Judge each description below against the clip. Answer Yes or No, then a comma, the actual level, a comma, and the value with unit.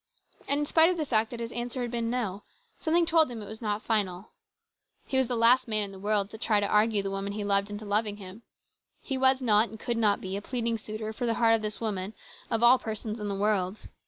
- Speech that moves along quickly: Yes, fast, 255 wpm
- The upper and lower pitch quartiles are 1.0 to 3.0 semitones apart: Yes, narrow, 2.6 semitones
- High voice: Yes, high, 220 Hz